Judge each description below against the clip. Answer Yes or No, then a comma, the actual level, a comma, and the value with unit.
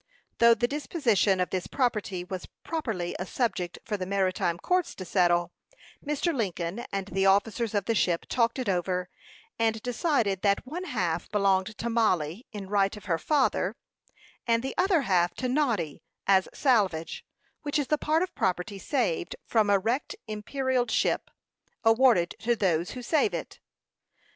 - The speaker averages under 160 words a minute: No, average, 165 wpm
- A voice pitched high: Yes, high, 210 Hz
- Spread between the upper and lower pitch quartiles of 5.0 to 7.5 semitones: Yes, wide, 5.4 semitones